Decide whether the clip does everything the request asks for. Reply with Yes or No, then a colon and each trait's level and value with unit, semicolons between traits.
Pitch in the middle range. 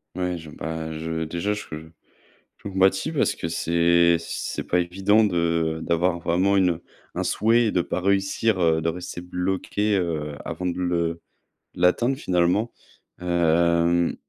No: very low, 85 Hz